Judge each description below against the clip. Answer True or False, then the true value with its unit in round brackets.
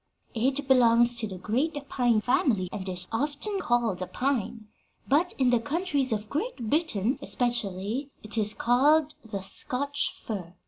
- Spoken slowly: False (150 wpm)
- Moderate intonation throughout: True (5.0 semitones)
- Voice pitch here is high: True (240 Hz)